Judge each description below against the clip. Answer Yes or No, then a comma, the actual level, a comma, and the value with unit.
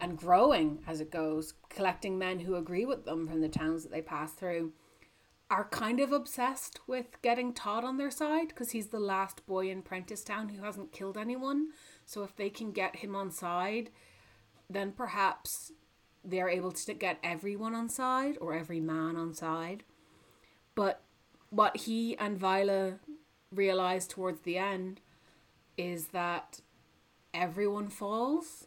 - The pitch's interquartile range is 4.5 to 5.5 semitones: Yes, average, 4.9 semitones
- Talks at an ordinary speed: Yes, average, 155 wpm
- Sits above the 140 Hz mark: Yes, high, 190 Hz